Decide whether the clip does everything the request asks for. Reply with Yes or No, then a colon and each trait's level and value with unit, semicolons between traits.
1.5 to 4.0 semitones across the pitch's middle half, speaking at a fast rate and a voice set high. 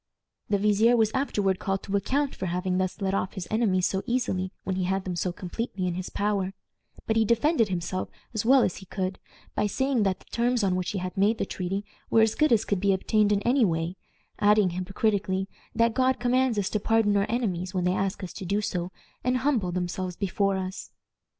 Yes: average, 3.2 semitones; fast, 220 wpm; high, 200 Hz